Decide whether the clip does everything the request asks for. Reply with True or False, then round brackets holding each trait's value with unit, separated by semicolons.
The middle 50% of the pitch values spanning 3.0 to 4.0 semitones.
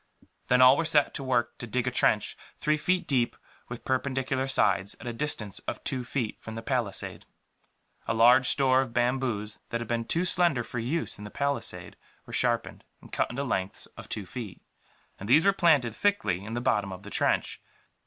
True (3.5 semitones)